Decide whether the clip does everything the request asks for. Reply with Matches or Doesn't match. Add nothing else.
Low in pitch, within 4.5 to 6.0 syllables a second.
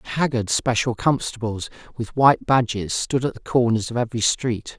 Matches